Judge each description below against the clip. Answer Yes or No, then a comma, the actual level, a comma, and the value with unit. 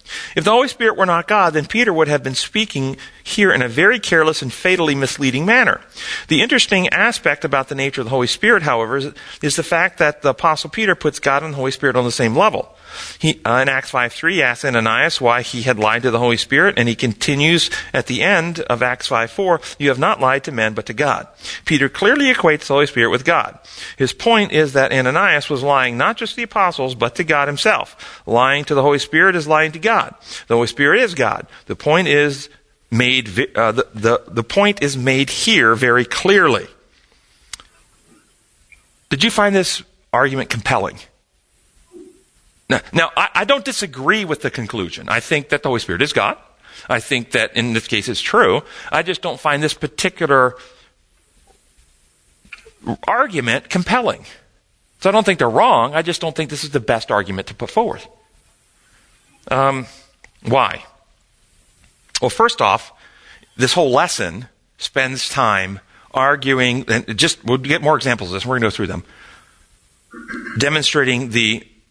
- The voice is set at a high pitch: No, medium, 140 Hz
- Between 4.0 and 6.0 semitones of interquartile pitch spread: Yes, average, 5.1 semitones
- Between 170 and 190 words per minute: Yes, average, 185 wpm